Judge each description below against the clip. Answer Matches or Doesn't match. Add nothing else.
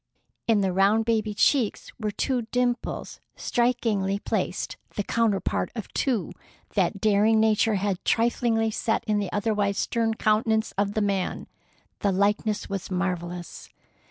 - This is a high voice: Matches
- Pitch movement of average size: Doesn't match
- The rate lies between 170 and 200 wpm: Doesn't match